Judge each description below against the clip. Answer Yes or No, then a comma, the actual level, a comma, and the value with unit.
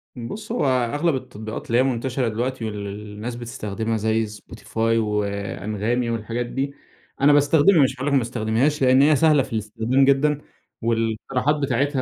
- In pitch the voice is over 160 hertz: No, low, 120 Hz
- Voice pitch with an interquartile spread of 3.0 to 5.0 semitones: Yes, average, 3.9 semitones